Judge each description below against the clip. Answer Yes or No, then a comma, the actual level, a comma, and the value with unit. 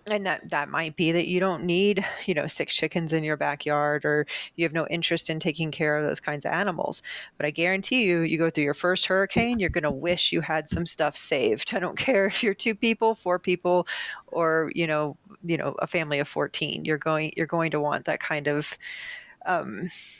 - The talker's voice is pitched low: No, medium, 170 Hz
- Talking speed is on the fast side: Yes, fast, 225 wpm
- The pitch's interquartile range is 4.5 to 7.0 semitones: No, average, 3.4 semitones